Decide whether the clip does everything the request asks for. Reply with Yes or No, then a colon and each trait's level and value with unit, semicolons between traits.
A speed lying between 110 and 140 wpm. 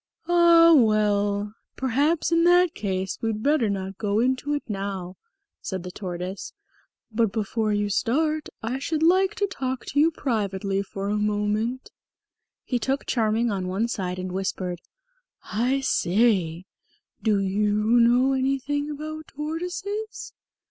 Yes: slow, 135 wpm